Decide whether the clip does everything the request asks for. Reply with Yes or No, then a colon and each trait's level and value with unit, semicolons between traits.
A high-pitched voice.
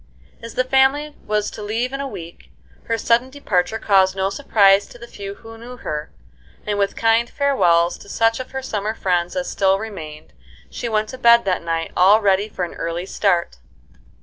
Yes: high, 210 Hz